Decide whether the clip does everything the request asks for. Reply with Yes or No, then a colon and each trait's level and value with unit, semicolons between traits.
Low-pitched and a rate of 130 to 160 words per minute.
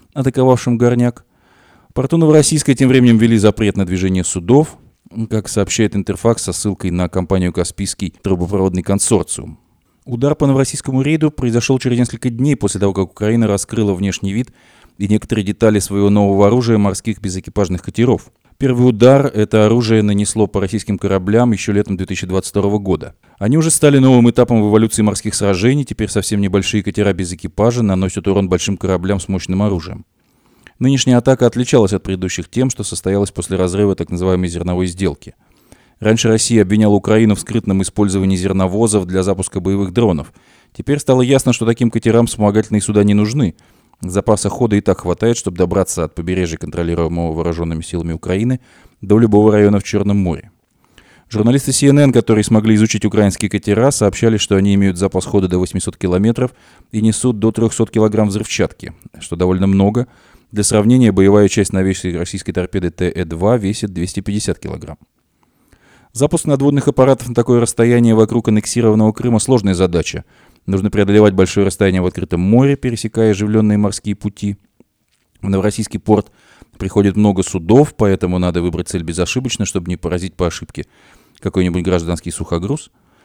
Yes: low, 105 Hz; average, 150 wpm